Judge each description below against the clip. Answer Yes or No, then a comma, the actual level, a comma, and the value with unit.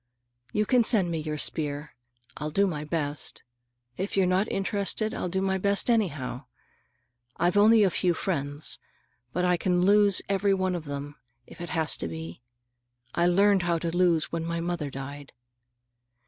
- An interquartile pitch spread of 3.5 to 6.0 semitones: Yes, average, 4.4 semitones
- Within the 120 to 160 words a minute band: No, average, 170 wpm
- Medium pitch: Yes, medium, 175 Hz